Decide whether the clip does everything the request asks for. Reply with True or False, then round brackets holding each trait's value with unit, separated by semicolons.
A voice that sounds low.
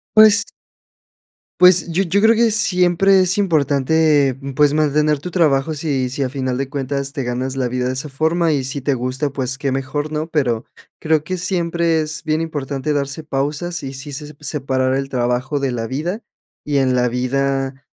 False (145 Hz)